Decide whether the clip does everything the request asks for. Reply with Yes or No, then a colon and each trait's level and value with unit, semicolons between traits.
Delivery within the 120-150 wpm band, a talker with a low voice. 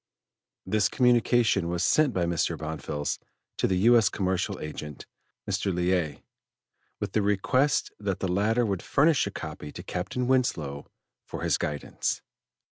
Yes: average, 145 wpm; very low, 95 Hz